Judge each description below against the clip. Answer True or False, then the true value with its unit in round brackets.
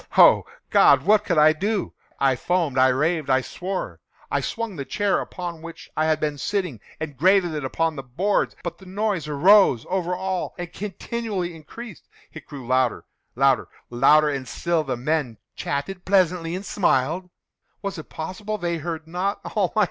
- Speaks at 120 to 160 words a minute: True (155 wpm)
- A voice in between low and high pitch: True (165 Hz)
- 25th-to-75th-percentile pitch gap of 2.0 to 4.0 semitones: False (4.6 semitones)